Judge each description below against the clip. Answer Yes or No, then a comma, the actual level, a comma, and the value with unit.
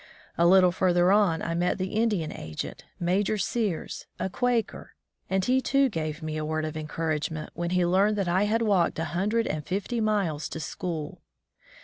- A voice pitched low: No, medium, 180 Hz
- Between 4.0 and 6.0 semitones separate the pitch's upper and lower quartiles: Yes, average, 4.5 semitones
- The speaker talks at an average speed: Yes, average, 185 wpm